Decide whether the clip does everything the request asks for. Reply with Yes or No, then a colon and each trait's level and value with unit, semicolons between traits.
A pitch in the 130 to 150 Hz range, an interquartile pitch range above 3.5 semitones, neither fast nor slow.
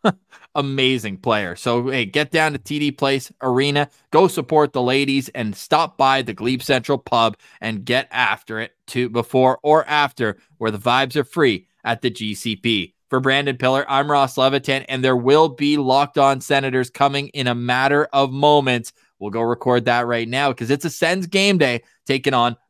No: low, 135 Hz; average, 3.0 semitones; average, 185 wpm